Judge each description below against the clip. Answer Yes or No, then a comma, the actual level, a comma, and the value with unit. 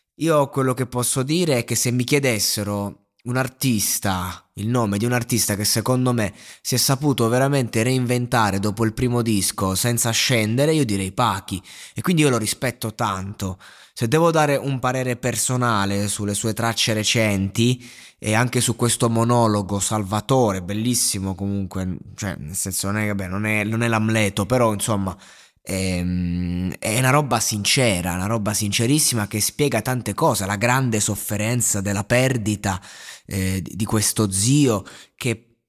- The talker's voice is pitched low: Yes, low, 110 Hz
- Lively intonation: No, average, 3.6 semitones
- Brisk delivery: No, average, 155 wpm